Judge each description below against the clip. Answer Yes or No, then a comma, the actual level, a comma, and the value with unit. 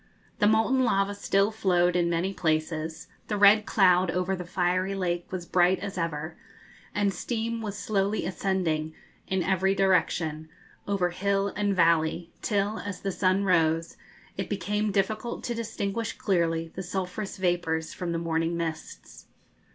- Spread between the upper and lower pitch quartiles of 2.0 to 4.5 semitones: Yes, average, 2.9 semitones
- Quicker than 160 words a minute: No, average, 150 wpm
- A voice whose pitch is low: No, medium, 185 Hz